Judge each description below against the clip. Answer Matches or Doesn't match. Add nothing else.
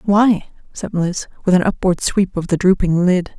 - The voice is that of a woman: Matches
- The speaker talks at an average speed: Matches